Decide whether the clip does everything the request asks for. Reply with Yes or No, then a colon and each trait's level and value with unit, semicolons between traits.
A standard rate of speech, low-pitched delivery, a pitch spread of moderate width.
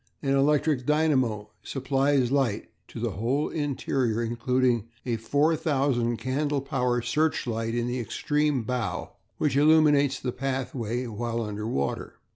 No: slow, 125 wpm; low, 130 Hz; average, 3.4 semitones